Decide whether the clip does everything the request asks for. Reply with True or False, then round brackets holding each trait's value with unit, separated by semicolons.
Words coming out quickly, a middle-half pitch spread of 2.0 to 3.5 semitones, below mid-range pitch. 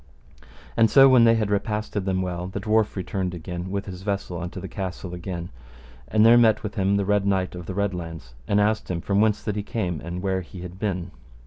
True (230 wpm; 2.7 semitones; 95 Hz)